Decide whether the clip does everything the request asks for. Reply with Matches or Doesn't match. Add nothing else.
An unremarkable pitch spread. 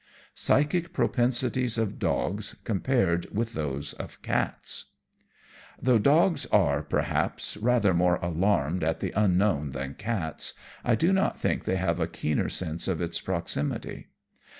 Doesn't match